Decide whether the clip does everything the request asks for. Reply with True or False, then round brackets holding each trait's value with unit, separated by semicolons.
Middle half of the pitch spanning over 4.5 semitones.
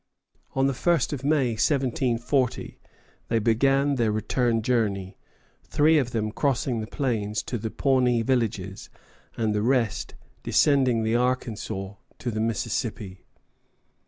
False (3.6 semitones)